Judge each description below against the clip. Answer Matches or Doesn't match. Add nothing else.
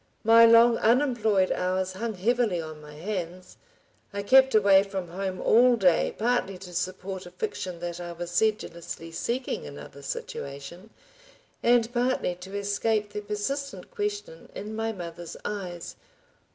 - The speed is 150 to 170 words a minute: Doesn't match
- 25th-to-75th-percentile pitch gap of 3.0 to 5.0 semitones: Matches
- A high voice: Matches